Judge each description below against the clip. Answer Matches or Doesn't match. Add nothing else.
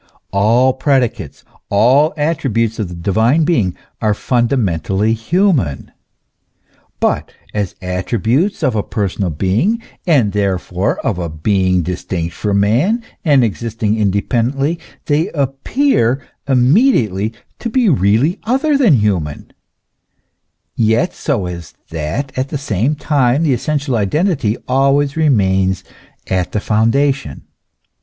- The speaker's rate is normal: Doesn't match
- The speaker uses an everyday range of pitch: Doesn't match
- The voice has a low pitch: Matches